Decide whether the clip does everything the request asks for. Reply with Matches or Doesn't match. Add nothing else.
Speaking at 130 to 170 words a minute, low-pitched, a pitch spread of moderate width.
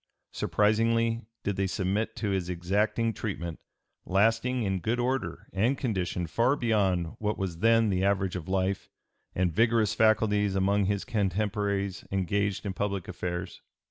Matches